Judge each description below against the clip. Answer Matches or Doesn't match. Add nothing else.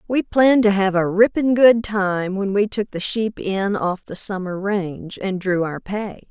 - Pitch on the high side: Matches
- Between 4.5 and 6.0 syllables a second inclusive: Doesn't match